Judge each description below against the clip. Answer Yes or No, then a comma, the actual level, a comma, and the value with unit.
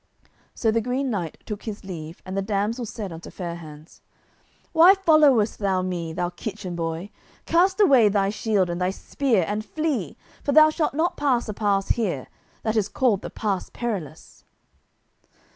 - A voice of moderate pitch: No, high, 210 Hz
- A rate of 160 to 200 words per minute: Yes, average, 170 wpm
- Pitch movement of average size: No, wide, 5.7 semitones